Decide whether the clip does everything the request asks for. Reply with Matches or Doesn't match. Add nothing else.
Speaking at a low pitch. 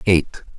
Matches